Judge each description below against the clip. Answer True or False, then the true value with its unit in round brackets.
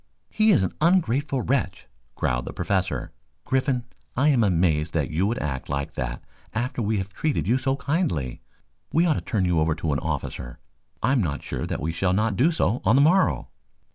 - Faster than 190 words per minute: True (200 wpm)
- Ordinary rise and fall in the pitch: False (8.8 semitones)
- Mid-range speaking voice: False (110 Hz)